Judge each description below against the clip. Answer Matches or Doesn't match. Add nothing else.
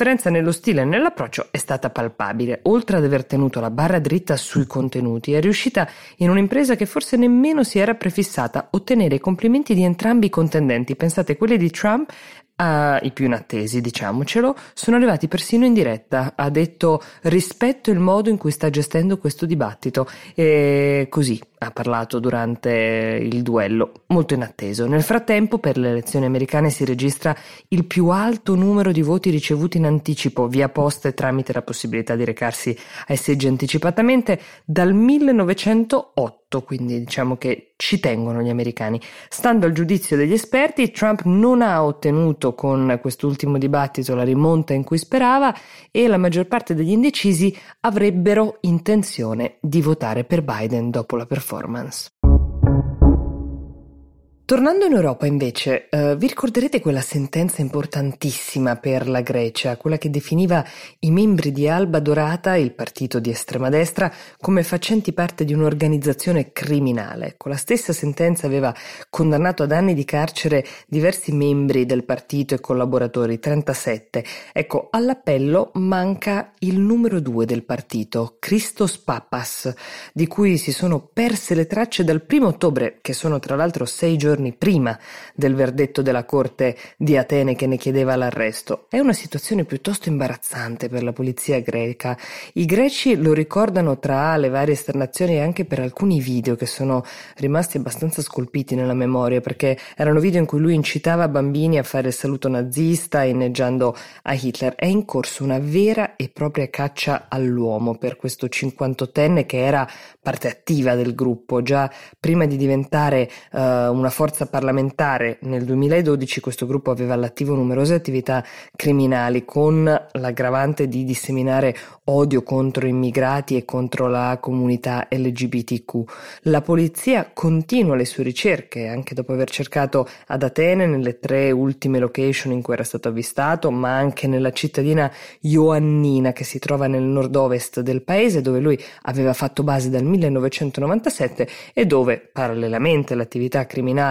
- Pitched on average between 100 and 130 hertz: Doesn't match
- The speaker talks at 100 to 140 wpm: Doesn't match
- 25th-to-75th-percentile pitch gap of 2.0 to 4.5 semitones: Doesn't match